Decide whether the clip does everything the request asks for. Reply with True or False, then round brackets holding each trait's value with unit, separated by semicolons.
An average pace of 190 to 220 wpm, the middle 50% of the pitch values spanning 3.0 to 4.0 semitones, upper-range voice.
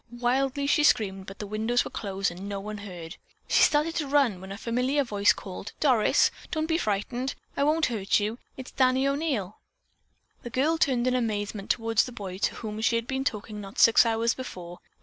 False (200 wpm; 4.6 semitones; 230 Hz)